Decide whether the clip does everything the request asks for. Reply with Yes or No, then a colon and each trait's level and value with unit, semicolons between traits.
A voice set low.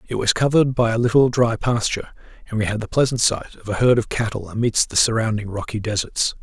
Yes: low, 115 Hz